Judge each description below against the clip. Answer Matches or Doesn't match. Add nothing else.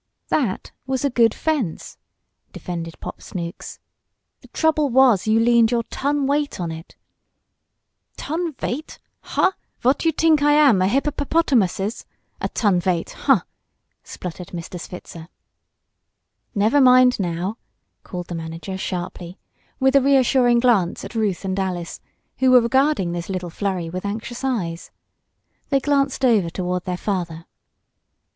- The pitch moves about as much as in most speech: Doesn't match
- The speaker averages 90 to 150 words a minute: Matches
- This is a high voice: Matches